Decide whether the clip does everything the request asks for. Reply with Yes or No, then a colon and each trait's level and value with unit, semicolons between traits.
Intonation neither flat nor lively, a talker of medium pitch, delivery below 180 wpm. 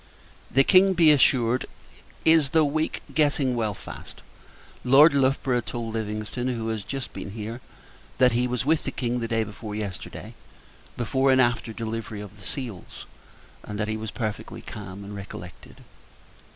No: average, 3.9 semitones; low, 120 Hz; average, 160 wpm